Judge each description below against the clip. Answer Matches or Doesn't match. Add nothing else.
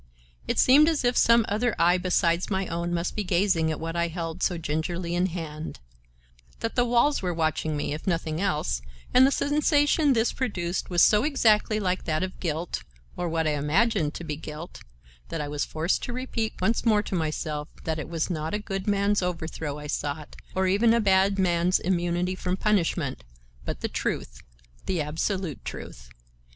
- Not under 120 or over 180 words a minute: Doesn't match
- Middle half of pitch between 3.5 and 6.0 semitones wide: Matches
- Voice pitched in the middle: Matches